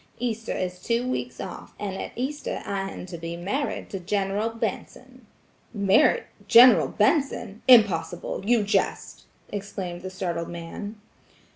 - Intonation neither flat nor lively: Yes, average, 4.2 semitones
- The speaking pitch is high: Yes, high, 200 Hz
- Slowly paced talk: Yes, slow, 130 wpm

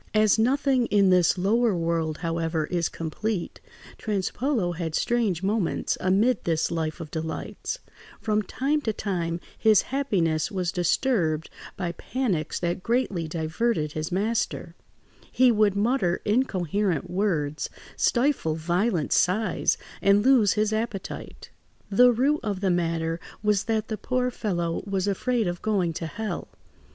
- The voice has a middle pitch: No, high, 195 Hz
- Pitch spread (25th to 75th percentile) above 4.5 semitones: Yes, average, 5.0 semitones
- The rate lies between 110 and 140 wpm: Yes, slow, 135 wpm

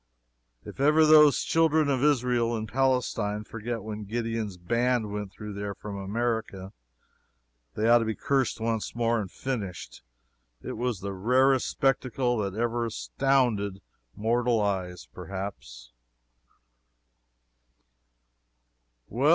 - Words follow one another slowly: Yes, slow, 115 wpm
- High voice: No, low, 115 Hz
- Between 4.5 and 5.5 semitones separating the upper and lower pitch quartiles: No, average, 3.6 semitones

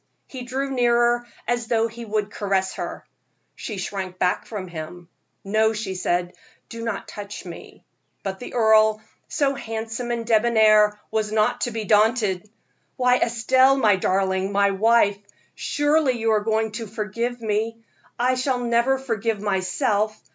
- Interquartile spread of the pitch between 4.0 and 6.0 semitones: No, average, 2.8 semitones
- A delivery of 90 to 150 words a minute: Yes, average, 145 wpm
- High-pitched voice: Yes, high, 220 Hz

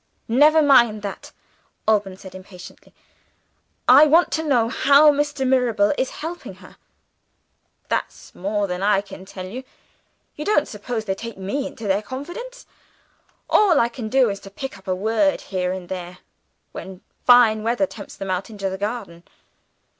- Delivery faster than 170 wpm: No, average, 160 wpm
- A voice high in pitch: Yes, high, 220 Hz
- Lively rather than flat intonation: Yes, wide, 6.2 semitones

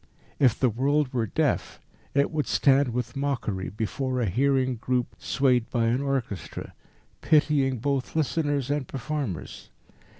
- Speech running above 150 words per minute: No, slow, 135 wpm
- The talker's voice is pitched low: Yes, low, 130 Hz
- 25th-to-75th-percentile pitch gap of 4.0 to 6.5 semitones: No, average, 2.7 semitones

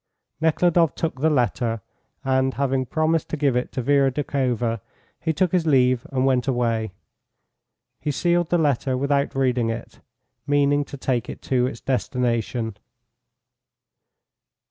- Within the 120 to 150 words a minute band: Yes, average, 140 wpm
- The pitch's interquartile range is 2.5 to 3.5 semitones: Yes, average, 2.9 semitones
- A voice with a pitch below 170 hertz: Yes, low, 135 Hz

